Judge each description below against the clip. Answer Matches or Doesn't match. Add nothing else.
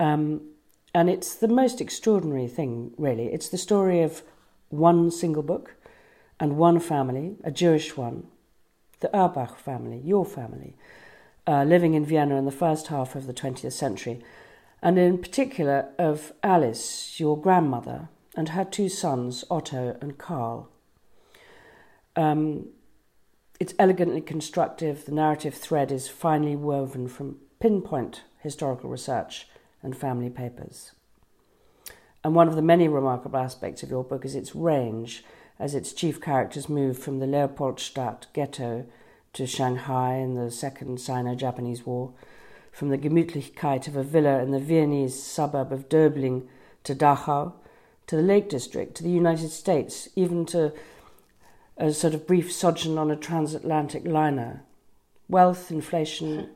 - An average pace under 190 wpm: Matches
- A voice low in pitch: Doesn't match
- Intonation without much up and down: Doesn't match